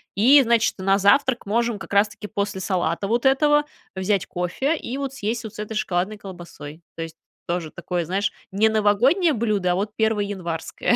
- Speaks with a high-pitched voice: Yes, high, 205 Hz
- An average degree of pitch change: Yes, average, 3.9 semitones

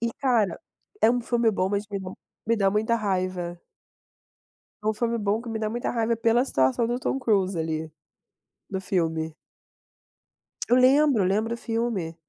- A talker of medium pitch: No, high, 215 Hz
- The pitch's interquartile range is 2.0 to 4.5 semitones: Yes, average, 4.0 semitones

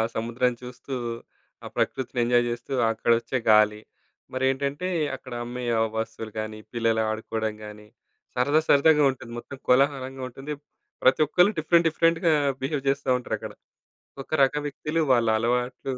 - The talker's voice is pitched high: No, low, 130 Hz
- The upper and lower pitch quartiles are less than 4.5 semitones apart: Yes, average, 3.4 semitones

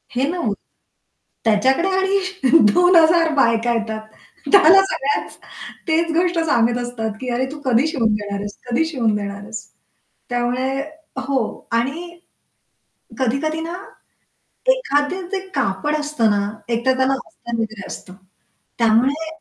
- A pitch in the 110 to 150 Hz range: No, very high, 265 Hz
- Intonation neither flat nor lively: No, wide, 6.0 semitones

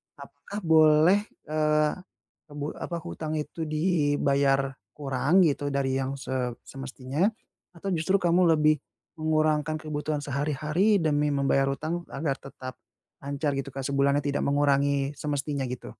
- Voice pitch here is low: No, medium, 145 Hz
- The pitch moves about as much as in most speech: No, narrow, 2.2 semitones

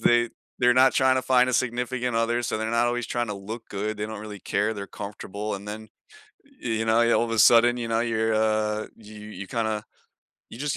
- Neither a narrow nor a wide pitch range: No, narrow, 2.0 semitones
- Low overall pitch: Yes, low, 115 Hz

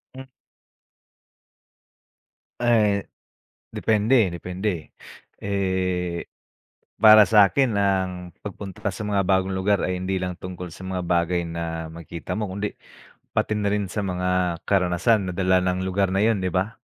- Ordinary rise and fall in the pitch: No, narrow, 2.2 semitones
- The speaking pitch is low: Yes, very low, 95 Hz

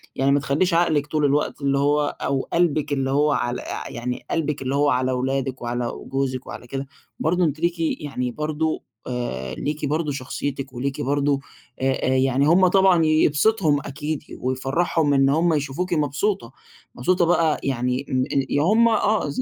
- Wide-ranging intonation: No, average, 3.0 semitones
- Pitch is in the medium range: Yes, medium, 145 Hz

